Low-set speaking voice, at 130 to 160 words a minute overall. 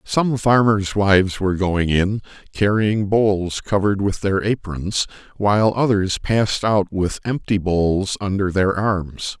Yes: low, 100 Hz; average, 140 wpm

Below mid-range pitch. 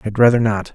Yes: low, 110 Hz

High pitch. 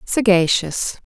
Yes: high, 195 Hz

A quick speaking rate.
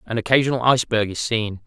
No: average, 180 wpm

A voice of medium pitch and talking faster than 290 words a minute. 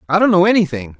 No: medium, 170 Hz; fast, 240 wpm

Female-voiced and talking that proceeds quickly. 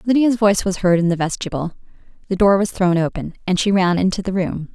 Yes: female; fast, 230 wpm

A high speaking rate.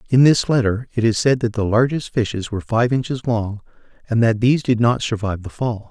Yes: fast, 225 wpm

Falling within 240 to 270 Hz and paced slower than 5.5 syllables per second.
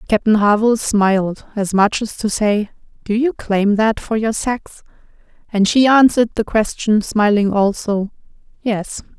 No: high, 215 Hz; 4.4 syllables/s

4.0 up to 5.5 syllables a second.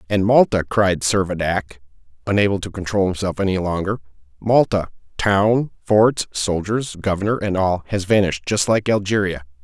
Yes: 5.0 syllables/s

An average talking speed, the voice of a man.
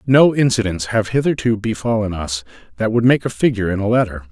Yes: average, 195 wpm; male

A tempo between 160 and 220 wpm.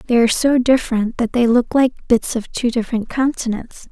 Yes: average, 200 wpm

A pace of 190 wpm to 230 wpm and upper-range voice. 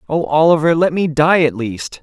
No: fast, 205 wpm; medium, 155 Hz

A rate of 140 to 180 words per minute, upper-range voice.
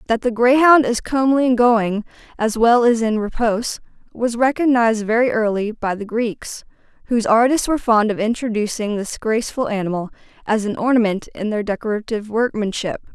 Yes: average, 160 wpm; high, 225 Hz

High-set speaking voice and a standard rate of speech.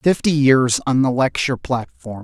No: low, 130 Hz; average, 160 wpm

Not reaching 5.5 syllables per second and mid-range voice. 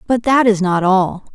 No: 4.4 syllables/s; high, 205 Hz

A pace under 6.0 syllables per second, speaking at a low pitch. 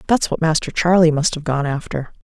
No: 5.6 syllables/s; medium, 160 Hz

